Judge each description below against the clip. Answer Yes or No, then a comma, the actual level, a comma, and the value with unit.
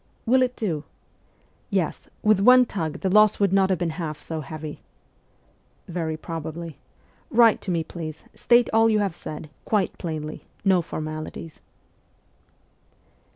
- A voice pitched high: No, medium, 175 Hz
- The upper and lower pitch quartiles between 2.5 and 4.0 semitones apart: No, average, 5.1 semitones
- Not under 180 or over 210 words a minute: No, average, 145 wpm